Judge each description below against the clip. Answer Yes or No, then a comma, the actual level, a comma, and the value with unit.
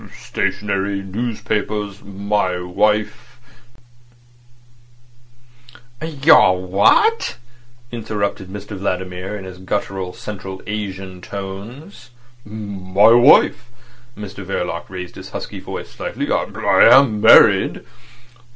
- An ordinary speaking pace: No, slow, 85 wpm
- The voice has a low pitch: Yes, low, 100 Hz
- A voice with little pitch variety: Yes, narrow, 2.3 semitones